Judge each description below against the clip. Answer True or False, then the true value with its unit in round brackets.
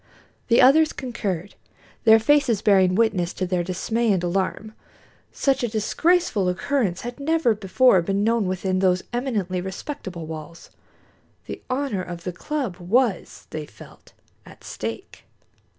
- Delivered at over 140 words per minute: False (135 wpm)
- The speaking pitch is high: True (205 Hz)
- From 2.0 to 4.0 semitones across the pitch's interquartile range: False (5.2 semitones)